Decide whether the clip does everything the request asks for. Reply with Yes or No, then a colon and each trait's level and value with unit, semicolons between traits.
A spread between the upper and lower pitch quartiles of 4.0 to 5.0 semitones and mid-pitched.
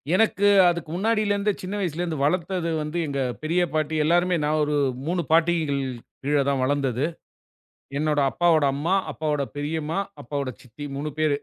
No: average, 3.2 semitones; medium, 155 Hz